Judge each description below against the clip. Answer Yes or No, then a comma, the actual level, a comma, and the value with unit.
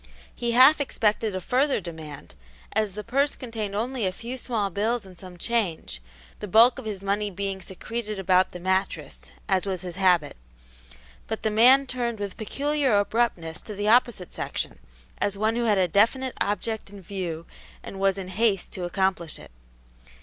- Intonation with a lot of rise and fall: No, average, 3.9 semitones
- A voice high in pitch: Yes, high, 205 Hz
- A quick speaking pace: No, average, 175 wpm